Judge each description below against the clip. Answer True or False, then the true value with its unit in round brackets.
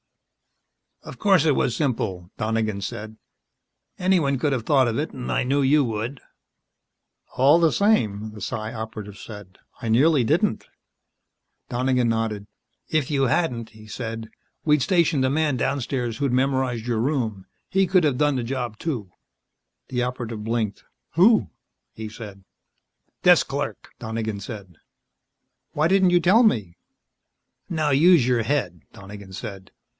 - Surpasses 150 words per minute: False (145 wpm)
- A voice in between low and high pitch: False (125 Hz)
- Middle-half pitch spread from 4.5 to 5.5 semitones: True (5.0 semitones)